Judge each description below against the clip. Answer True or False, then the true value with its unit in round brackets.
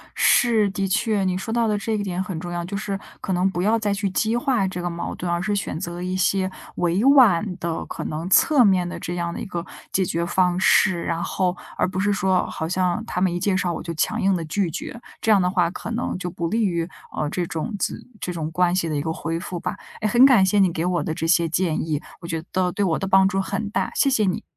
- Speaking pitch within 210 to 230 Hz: False (185 Hz)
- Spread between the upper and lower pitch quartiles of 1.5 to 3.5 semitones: True (2.8 semitones)